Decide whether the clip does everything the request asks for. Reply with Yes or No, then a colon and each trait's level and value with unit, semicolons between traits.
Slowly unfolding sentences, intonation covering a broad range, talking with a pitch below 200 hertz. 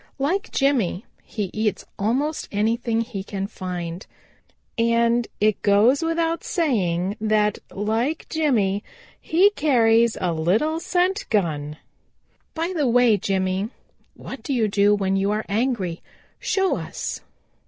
No: slow, 125 wpm; wide, 5.8 semitones; high, 220 Hz